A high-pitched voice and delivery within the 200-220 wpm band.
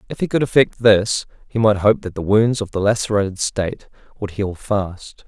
No: low, 105 Hz; fast, 205 wpm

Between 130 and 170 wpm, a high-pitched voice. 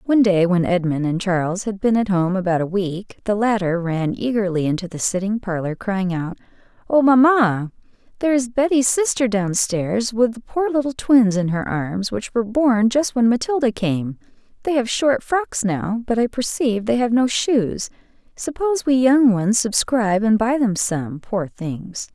No: average, 185 wpm; high, 215 Hz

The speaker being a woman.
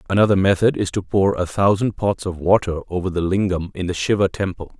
No: male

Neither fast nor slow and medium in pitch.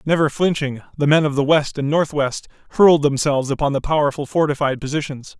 Yes: average, 180 wpm; medium, 145 Hz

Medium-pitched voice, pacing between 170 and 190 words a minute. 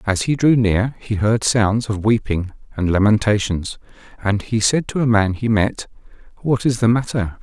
No: low, 110 Hz; average, 185 wpm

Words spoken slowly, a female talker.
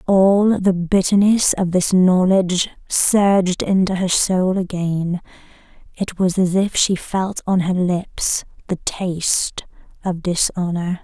Yes: slow, 130 wpm; female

